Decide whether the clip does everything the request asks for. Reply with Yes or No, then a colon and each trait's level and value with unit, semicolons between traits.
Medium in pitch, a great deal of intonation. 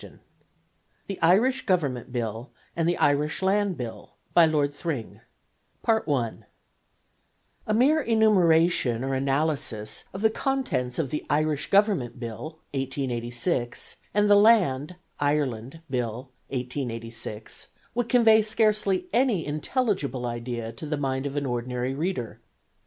Yes: medium, 145 Hz; wide, 7.7 semitones